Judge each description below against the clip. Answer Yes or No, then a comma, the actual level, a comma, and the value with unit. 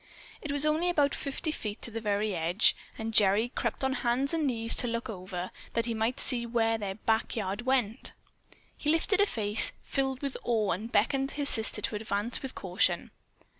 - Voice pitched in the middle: No, high, 230 Hz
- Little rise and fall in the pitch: No, average, 4.3 semitones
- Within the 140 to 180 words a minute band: No, average, 195 wpm